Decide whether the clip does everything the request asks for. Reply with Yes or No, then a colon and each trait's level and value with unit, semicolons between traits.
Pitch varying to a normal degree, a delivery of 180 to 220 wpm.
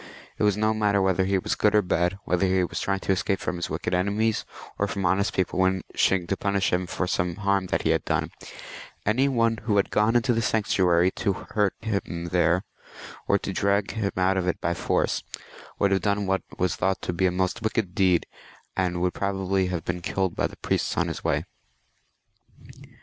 No: narrow, 2.0 semitones; fast, 205 wpm